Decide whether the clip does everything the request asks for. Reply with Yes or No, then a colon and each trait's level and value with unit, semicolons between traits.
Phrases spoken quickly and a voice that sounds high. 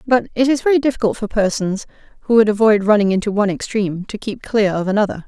Yes: fast, 215 wpm; high, 215 Hz